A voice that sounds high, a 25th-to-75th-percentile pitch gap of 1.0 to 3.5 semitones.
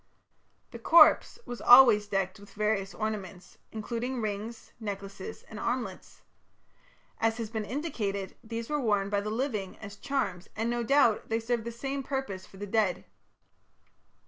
Yes: high, 220 Hz; average, 3.0 semitones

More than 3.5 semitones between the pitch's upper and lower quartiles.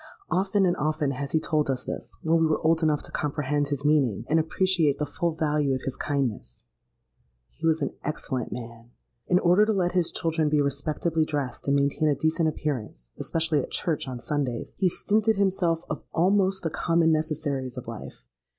No: average, 3.0 semitones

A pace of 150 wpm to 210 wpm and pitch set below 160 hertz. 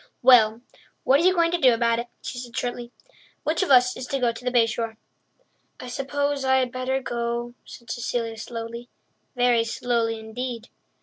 No: average, 180 wpm; high, 245 Hz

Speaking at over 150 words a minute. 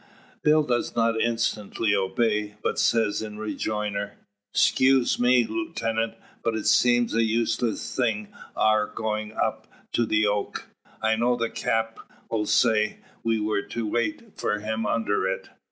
No: average, 140 wpm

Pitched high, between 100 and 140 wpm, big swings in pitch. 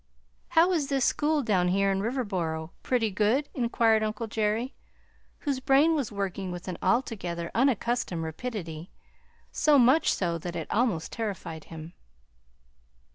Yes: high, 215 Hz; slow, 135 wpm; wide, 6.4 semitones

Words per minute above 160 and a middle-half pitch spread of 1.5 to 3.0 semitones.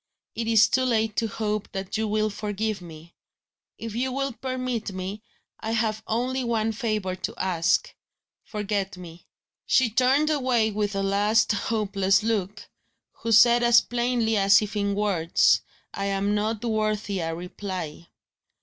No: average, 150 wpm; narrow, 2.6 semitones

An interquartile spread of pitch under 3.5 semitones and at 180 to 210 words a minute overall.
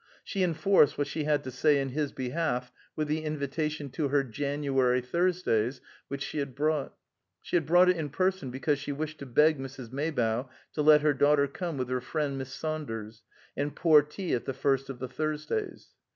Yes: average, 2.8 semitones; average, 195 wpm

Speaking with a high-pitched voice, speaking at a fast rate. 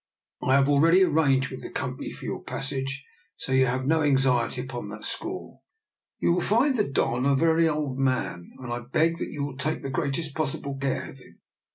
No: low, 135 Hz; fast, 225 wpm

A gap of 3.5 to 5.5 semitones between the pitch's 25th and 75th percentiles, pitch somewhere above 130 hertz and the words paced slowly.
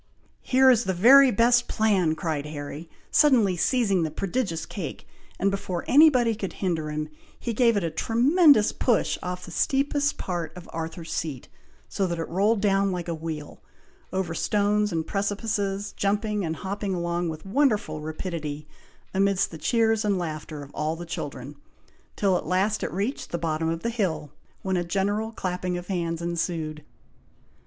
No: average, 4.5 semitones; medium, 185 Hz; average, 170 wpm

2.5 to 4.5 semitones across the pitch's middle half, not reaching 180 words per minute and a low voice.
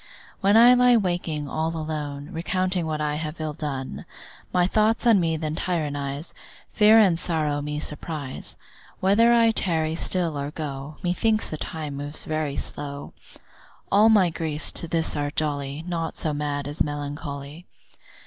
No: average, 3.6 semitones; average, 155 wpm; medium, 155 Hz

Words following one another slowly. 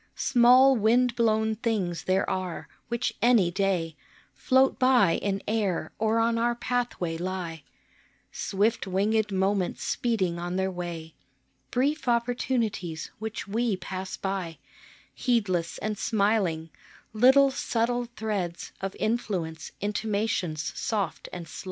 Yes: slow, 120 wpm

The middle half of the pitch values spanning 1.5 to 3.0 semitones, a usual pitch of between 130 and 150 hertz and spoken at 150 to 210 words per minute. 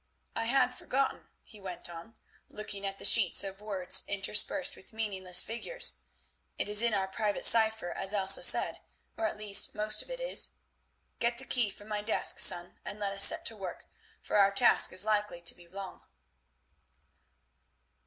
No: narrow, 2.5 semitones; high, 210 Hz; average, 175 wpm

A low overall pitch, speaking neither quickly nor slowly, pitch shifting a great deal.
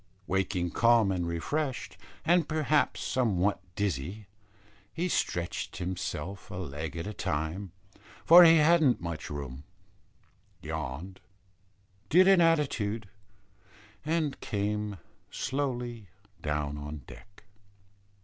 No: low, 100 Hz; slow, 100 wpm; wide, 8.6 semitones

